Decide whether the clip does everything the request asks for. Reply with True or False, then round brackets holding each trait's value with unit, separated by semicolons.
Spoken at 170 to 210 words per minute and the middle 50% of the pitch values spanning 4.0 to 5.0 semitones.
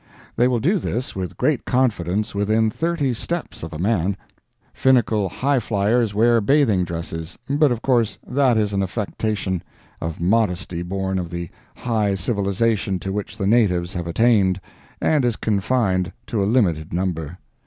False (155 wpm; 4.5 semitones)